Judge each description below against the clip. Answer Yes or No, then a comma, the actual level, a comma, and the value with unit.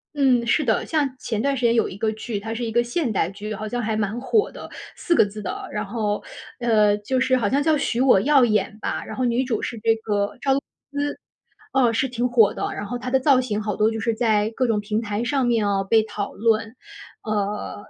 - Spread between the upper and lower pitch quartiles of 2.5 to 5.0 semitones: Yes, average, 3.1 semitones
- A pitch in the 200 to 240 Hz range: Yes, high, 225 Hz